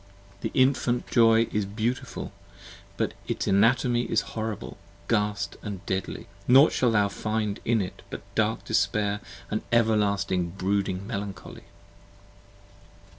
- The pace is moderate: No, slow, 115 wpm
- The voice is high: No, low, 105 Hz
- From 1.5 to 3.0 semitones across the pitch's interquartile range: Yes, average, 2.7 semitones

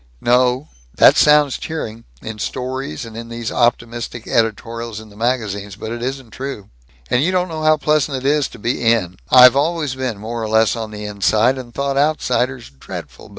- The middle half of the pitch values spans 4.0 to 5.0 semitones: No, average, 3.4 semitones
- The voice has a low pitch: Yes, low, 120 Hz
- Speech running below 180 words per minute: No, average, 185 wpm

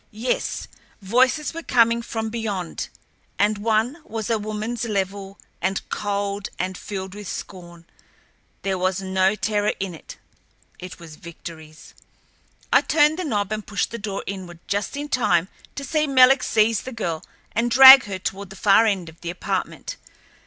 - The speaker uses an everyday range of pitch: Yes, average, 3.6 semitones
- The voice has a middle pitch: No, high, 205 Hz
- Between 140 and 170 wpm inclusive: Yes, average, 160 wpm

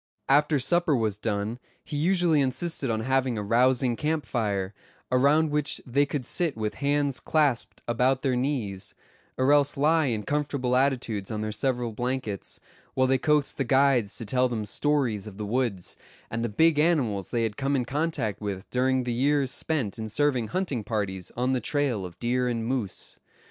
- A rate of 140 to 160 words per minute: No, average, 180 wpm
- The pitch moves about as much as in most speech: Yes, average, 4.5 semitones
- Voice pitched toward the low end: Yes, low, 130 Hz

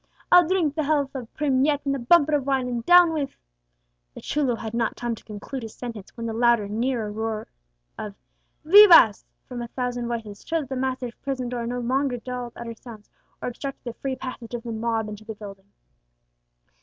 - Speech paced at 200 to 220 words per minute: Yes, fast, 205 wpm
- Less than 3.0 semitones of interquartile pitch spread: No, average, 3.4 semitones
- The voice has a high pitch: Yes, high, 245 Hz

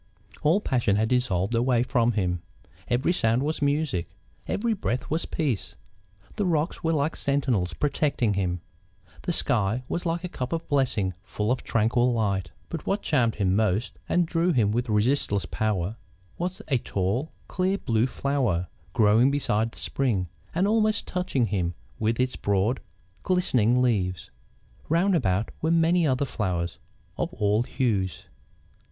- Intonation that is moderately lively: No, wide, 6.8 semitones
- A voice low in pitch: Yes, low, 125 Hz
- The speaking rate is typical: Yes, average, 150 wpm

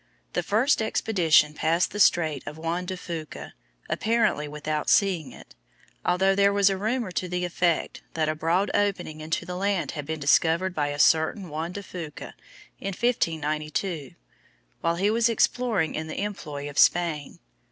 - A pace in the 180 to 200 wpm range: No, average, 165 wpm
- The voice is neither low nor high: Yes, medium, 175 Hz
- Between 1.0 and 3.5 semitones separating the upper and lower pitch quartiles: No, average, 4.1 semitones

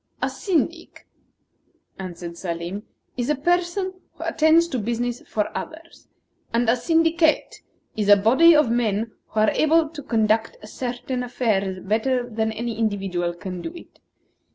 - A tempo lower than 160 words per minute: Yes, average, 145 wpm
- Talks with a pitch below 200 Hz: No, high, 240 Hz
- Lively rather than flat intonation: Yes, wide, 6.9 semitones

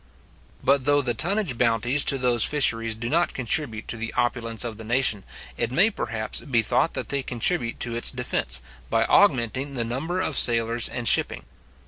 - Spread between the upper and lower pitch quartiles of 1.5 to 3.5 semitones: Yes, average, 3.2 semitones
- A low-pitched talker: Yes, low, 120 Hz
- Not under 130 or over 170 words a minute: No, average, 185 wpm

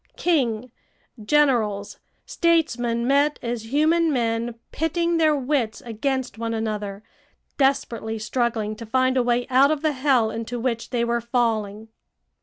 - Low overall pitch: No, high, 240 Hz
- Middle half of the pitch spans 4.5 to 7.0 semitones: No, average, 3.8 semitones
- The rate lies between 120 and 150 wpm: Yes, slow, 135 wpm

